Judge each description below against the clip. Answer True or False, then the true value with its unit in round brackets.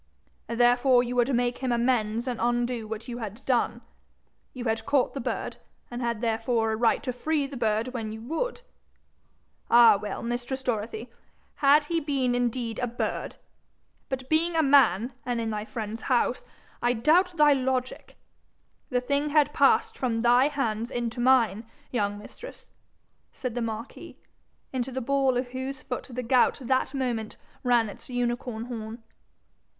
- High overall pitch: True (245 Hz)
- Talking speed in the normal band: True (160 wpm)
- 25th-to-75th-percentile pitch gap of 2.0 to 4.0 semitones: True (2.5 semitones)